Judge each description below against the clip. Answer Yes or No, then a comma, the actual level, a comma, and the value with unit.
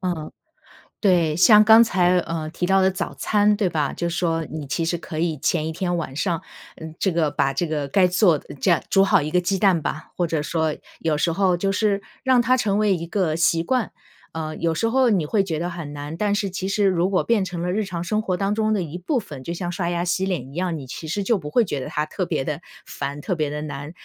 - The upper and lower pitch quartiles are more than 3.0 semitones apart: Yes, average, 3.8 semitones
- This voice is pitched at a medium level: Yes, medium, 175 Hz